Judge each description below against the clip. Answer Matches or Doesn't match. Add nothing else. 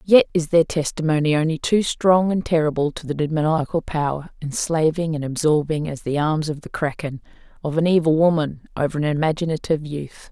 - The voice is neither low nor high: Matches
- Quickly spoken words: Doesn't match